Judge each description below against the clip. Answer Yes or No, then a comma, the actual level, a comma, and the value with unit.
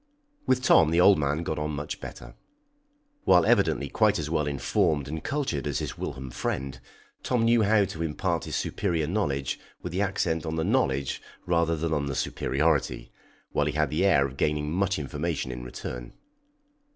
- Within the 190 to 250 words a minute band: No, average, 180 wpm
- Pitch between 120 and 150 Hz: No, very low, 80 Hz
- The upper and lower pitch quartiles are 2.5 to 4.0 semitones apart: No, average, 4.6 semitones